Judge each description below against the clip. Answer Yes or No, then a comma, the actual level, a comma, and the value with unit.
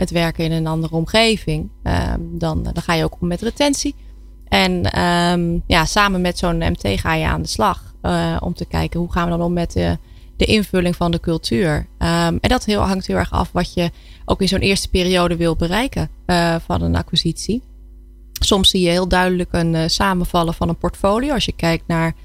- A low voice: No, medium, 170 Hz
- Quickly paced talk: Yes, fast, 215 wpm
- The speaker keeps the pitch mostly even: Yes, narrow, 2.2 semitones